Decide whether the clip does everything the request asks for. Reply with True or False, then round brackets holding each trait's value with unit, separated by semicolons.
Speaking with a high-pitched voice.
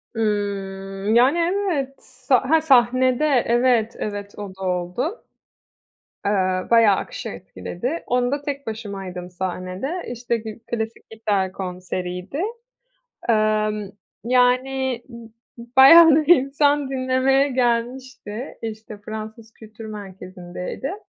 True (230 Hz)